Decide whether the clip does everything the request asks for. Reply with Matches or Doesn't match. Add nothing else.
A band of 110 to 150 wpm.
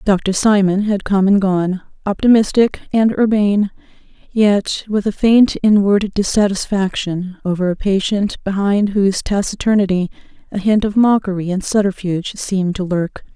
Matches